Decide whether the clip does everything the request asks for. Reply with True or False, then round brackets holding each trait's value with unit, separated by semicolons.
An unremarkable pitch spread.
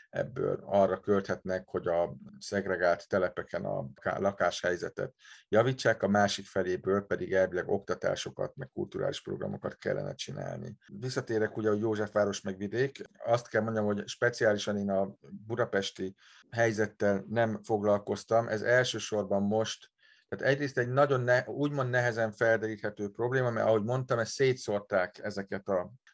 True (3.0 semitones)